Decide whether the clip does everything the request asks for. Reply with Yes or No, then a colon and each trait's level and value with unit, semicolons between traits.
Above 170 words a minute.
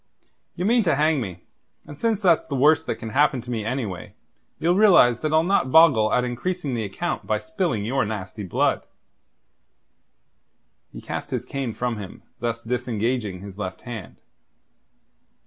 No: average, 165 wpm